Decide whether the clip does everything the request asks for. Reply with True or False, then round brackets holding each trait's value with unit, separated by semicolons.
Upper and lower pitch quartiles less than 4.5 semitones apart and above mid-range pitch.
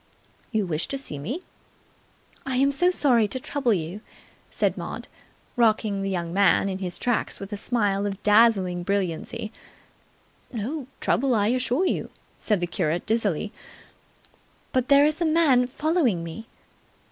False (5.1 semitones; 220 Hz)